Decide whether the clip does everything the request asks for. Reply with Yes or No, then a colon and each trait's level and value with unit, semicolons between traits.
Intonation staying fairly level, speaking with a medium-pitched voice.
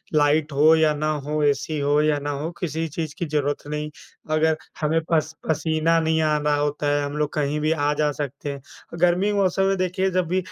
Yes: narrow, 1.7 semitones; medium, 155 Hz